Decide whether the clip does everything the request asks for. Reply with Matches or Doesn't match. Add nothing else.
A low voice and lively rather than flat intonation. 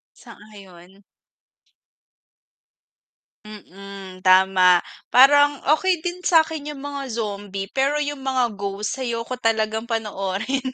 Doesn't match